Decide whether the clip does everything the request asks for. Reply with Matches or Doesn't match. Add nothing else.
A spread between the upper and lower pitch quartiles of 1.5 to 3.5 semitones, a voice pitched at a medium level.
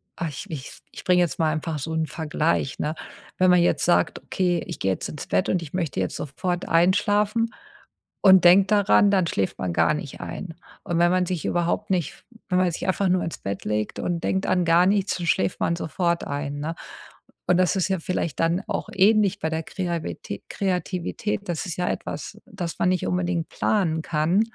Matches